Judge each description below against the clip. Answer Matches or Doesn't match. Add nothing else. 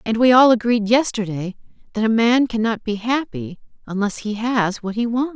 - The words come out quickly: Doesn't match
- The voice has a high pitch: Matches